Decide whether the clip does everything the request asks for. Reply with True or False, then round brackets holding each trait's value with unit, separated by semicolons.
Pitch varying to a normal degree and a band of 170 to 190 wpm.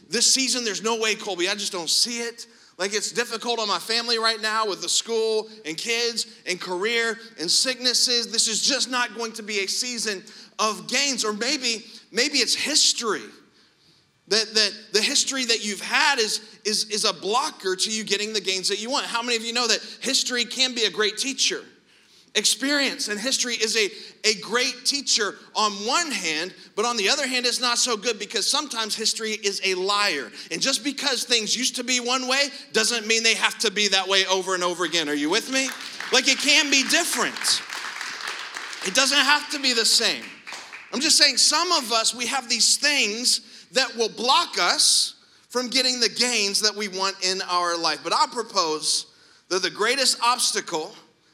False (3.3 semitones; 200 wpm)